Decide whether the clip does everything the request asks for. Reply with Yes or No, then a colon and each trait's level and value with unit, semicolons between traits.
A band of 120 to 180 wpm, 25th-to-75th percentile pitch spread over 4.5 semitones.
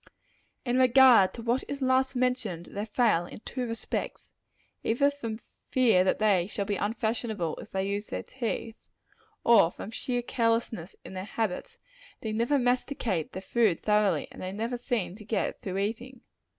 No: average, 165 wpm; average, 3.7 semitones